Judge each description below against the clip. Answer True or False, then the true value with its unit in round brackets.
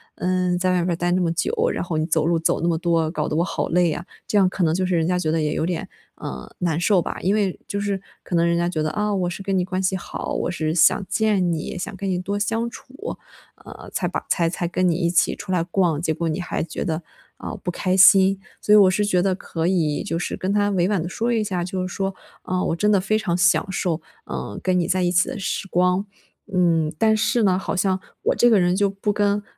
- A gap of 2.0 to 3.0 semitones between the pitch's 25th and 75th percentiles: True (2.4 semitones)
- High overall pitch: False (180 Hz)